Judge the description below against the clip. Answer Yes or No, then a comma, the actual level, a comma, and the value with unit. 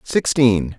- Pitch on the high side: No, low, 115 Hz